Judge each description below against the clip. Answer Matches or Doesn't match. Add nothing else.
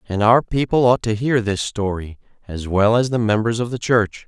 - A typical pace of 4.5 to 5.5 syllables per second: Matches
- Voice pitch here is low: Matches